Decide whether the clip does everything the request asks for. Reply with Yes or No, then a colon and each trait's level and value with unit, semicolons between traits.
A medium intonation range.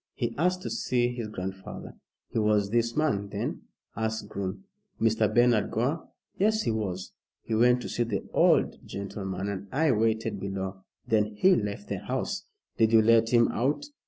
Yes: average, 3.2 semitones